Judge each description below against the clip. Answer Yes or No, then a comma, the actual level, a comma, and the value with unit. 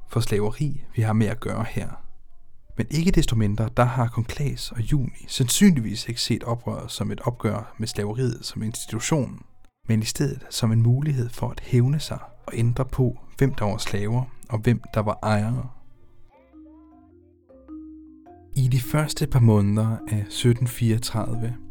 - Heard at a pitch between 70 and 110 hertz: No, low, 120 Hz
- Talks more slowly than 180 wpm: Yes, average, 160 wpm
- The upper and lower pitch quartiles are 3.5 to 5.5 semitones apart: No, average, 3.1 semitones